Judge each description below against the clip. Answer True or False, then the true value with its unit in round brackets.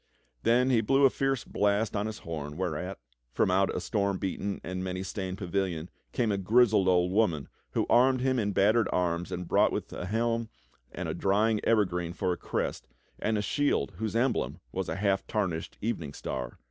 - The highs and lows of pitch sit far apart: False (3.7 semitones)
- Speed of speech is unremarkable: True (190 wpm)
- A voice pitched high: False (100 Hz)